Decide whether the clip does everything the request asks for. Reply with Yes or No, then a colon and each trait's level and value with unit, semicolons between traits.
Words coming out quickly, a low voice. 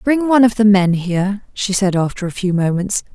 No: fast, 230 wpm; high, 200 Hz